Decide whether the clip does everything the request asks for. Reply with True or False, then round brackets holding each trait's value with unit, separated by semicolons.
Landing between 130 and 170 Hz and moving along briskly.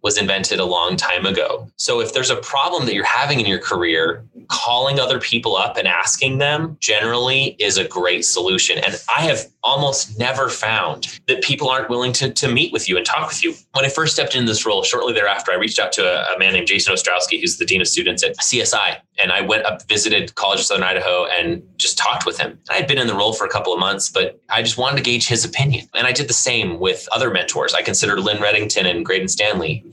True (140 Hz; 245 wpm)